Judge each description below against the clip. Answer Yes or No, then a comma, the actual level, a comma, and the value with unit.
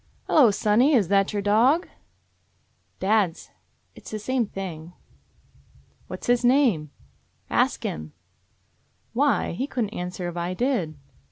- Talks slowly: Yes, slow, 120 wpm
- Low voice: No, high, 210 Hz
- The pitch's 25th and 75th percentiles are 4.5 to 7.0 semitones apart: Yes, wide, 5.6 semitones